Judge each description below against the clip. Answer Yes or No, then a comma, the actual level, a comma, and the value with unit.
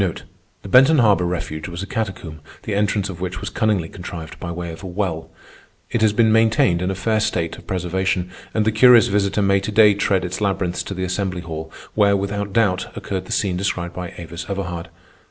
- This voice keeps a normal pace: No, fast, 210 wpm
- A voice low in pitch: Yes, very low, 95 Hz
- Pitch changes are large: No, average, 2.7 semitones